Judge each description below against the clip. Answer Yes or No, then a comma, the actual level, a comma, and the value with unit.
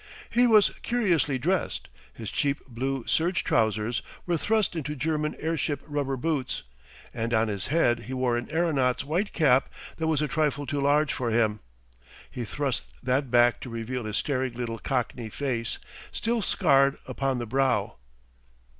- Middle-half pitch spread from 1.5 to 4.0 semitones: No, average, 4.4 semitones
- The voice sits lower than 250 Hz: Yes, low, 135 Hz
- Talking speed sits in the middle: Yes, average, 160 wpm